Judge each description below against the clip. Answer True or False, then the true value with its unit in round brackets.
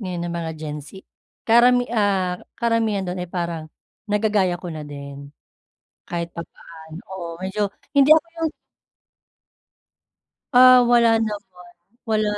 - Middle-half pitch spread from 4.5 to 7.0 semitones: True (4.9 semitones)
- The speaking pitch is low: False (190 Hz)